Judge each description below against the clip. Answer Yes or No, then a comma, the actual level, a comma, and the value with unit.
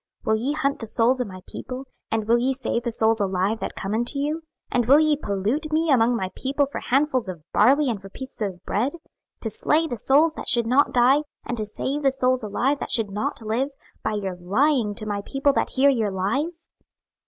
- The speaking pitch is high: Yes, high, 245 Hz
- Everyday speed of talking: No, fast, 225 wpm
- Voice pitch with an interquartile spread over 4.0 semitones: Yes, average, 4.7 semitones